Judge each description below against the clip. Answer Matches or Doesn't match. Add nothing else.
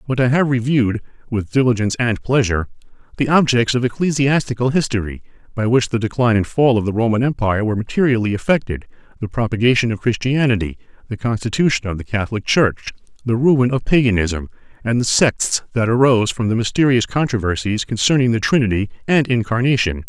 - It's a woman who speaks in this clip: Doesn't match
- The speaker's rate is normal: Matches